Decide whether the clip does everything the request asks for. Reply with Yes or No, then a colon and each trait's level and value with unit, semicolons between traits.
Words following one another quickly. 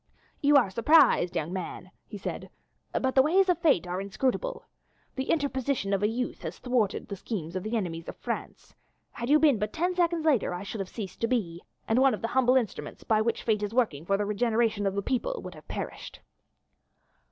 Yes: fast, 210 wpm